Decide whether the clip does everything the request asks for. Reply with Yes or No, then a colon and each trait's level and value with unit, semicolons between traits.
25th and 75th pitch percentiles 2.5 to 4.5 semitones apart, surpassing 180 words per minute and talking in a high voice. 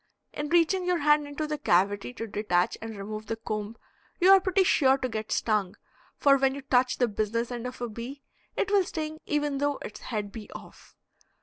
No: wide, 5.5 semitones; fast, 205 wpm; very high, 255 Hz